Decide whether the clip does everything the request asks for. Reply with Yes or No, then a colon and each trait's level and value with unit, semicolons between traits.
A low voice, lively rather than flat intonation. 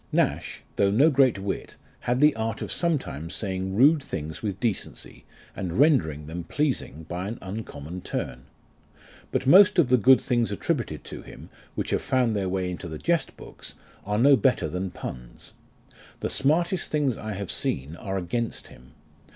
Yes: low, 105 Hz; wide, 7.2 semitones